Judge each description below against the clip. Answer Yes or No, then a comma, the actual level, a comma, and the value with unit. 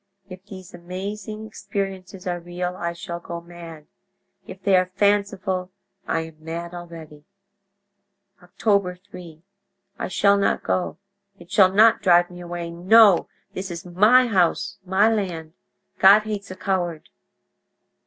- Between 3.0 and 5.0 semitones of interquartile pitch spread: No, narrow, 2.5 semitones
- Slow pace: Yes, slow, 130 wpm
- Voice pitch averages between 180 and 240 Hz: Yes, medium, 185 Hz